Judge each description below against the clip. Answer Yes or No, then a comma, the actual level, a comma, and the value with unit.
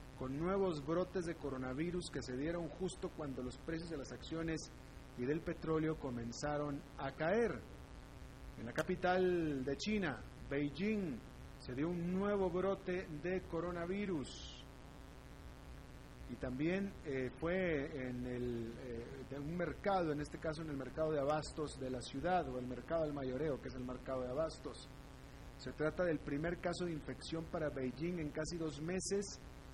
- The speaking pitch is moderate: Yes, medium, 155 Hz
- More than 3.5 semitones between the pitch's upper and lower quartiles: Yes, average, 4.6 semitones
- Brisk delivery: No, average, 160 wpm